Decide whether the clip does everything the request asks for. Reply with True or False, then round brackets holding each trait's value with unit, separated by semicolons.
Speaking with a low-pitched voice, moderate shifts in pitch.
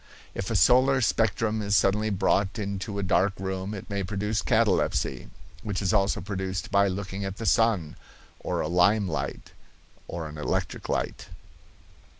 False (100 Hz; 2.0 semitones)